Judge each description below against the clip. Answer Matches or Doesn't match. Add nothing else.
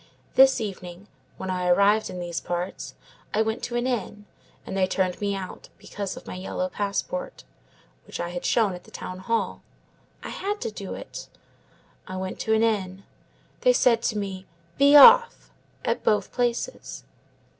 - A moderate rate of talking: Matches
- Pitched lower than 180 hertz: Doesn't match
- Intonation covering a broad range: Doesn't match